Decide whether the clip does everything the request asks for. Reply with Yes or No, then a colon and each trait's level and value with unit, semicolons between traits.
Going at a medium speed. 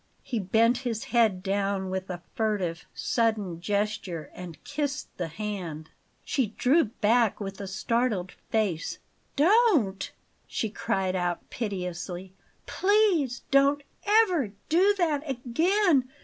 No: slow, 120 wpm